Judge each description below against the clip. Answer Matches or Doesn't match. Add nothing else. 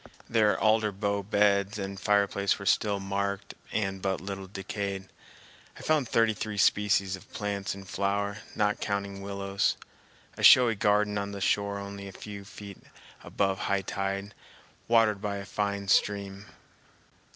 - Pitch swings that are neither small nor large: Doesn't match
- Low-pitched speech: Matches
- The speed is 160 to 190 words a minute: Doesn't match